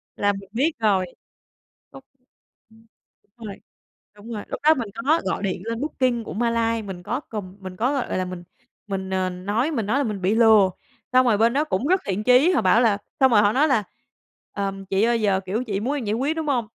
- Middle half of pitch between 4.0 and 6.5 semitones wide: Yes, average, 4.3 semitones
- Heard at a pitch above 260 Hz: No, high, 225 Hz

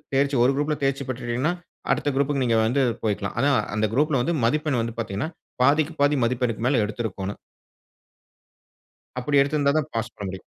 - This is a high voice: No, low, 130 Hz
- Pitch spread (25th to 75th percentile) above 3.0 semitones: Yes, average, 4.0 semitones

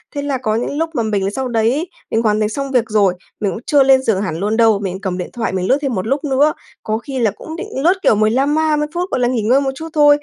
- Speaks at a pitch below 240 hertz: No, high, 245 Hz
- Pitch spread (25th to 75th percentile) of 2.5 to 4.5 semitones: No, average, 4.9 semitones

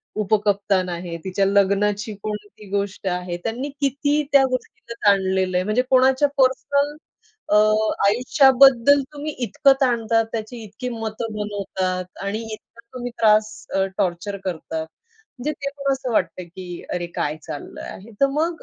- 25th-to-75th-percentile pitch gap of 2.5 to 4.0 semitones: No, average, 5.2 semitones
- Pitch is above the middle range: Yes, high, 215 Hz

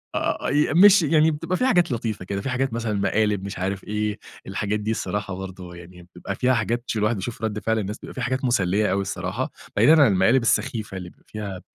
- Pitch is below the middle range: Yes, low, 105 Hz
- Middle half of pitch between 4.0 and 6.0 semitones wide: Yes, average, 4.3 semitones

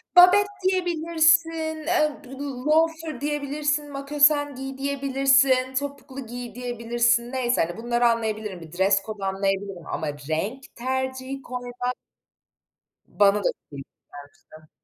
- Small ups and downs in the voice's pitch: No, average, 4.3 semitones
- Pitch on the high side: Yes, very high, 260 Hz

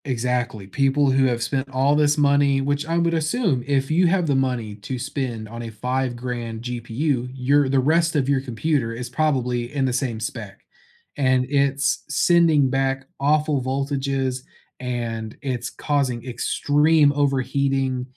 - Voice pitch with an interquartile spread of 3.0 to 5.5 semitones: No, narrow, 2.6 semitones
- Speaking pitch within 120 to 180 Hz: Yes, low, 135 Hz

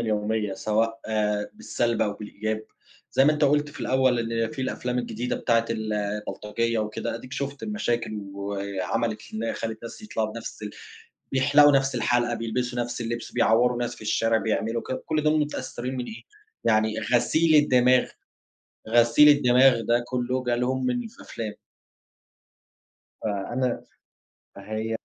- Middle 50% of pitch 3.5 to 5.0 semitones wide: No, average, 2.8 semitones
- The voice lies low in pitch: Yes, low, 120 Hz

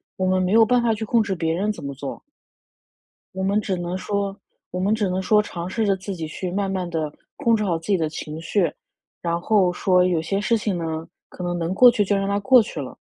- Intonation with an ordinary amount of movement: Yes, average, 3.3 semitones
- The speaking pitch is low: No, high, 190 Hz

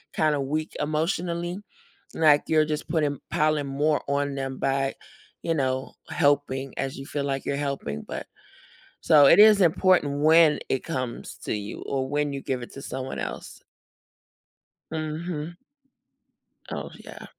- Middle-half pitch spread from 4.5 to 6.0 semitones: No, narrow, 2.5 semitones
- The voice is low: No, medium, 145 Hz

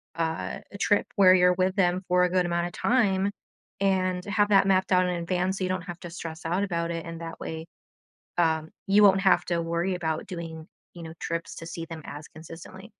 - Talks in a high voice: No, medium, 180 Hz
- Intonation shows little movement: Yes, narrow, 2.2 semitones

